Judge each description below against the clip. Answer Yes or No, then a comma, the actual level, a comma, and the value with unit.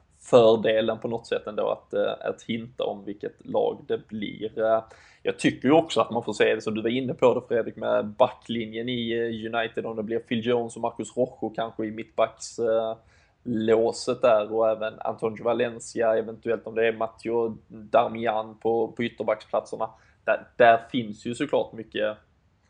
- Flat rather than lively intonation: Yes, narrow, 1.1 semitones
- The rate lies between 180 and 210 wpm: No, average, 170 wpm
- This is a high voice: No, low, 115 Hz